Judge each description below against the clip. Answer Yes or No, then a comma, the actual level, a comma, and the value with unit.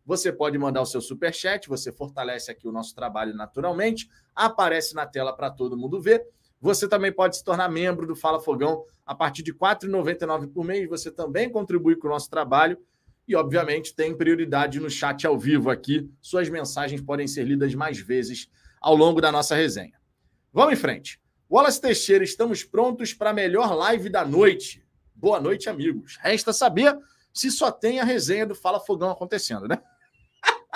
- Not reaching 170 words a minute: No, average, 180 wpm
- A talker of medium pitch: Yes, medium, 170 Hz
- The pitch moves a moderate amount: No, wide, 6.2 semitones